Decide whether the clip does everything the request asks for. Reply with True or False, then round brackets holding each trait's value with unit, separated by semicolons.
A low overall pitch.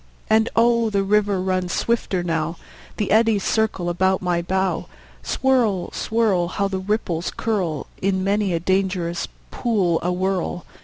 False (190 Hz)